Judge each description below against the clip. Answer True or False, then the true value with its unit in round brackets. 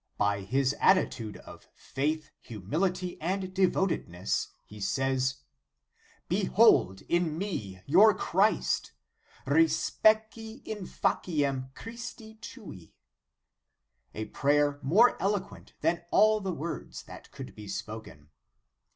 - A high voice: False (155 Hz)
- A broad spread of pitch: True (8.1 semitones)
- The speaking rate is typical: False (100 wpm)